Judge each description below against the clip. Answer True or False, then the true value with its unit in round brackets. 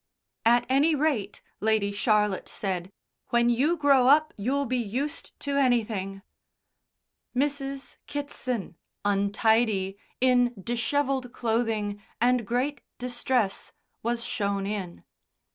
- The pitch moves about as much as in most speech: True (4.6 semitones)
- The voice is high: True (240 Hz)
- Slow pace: True (105 wpm)